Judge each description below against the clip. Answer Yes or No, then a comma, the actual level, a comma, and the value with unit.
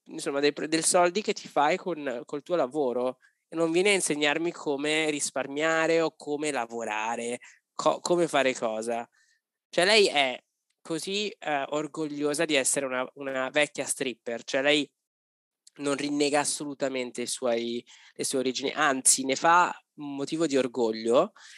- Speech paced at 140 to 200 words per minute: Yes, average, 150 wpm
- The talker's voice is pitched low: No, medium, 145 Hz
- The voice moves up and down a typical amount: Yes, average, 3.8 semitones